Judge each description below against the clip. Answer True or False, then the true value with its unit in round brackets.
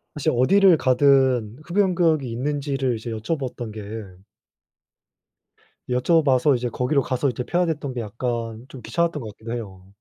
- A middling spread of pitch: True (4.1 semitones)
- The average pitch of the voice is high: False (130 Hz)